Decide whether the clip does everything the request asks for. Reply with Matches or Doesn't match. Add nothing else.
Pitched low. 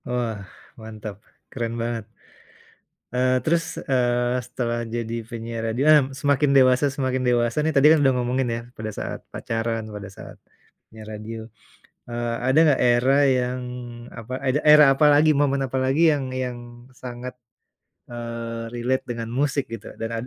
Matches